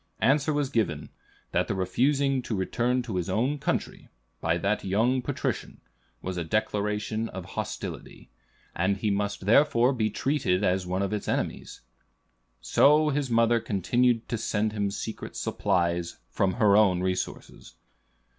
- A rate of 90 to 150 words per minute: Yes, average, 145 wpm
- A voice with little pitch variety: No, average, 4.7 semitones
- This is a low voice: Yes, low, 105 Hz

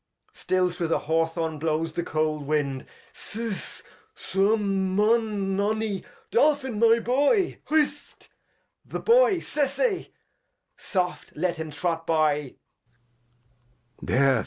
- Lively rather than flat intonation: Yes, wide, 6.1 semitones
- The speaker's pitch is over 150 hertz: Yes, high, 190 Hz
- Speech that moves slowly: Yes, slow, 120 wpm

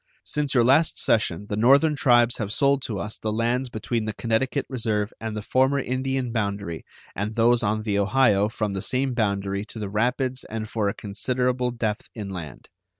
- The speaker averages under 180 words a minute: No, average, 185 wpm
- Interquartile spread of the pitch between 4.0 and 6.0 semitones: No, average, 3.4 semitones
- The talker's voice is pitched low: Yes, low, 115 Hz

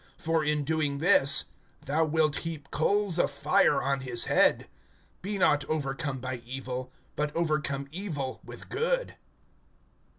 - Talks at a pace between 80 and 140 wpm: Yes, slow, 135 wpm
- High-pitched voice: No, medium, 150 Hz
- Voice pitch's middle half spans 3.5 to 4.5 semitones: No, average, 3.0 semitones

